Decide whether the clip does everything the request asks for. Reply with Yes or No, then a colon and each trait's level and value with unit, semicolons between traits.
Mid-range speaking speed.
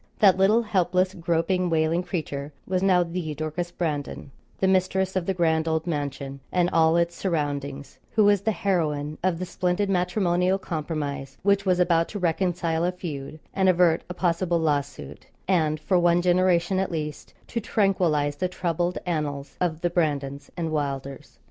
Yes: average, 165 wpm